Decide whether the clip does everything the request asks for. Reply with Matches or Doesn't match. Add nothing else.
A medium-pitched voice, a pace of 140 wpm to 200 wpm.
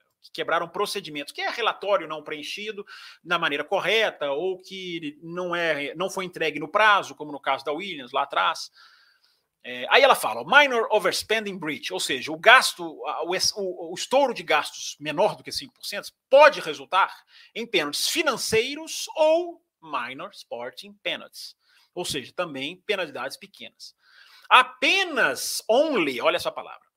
Doesn't match